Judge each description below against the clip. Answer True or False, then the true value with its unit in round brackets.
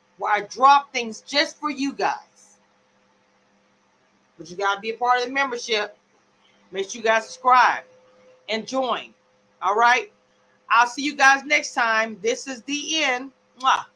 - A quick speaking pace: False (160 wpm)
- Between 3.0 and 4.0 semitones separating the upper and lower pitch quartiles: False (5.1 semitones)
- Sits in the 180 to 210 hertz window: False (240 Hz)